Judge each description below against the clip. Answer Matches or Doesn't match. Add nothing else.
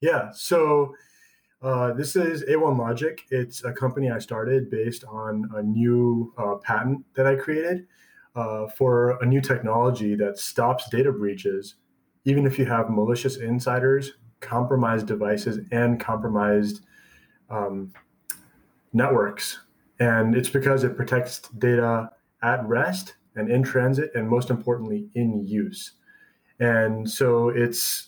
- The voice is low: Matches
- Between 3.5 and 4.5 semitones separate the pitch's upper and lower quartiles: Doesn't match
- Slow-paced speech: Matches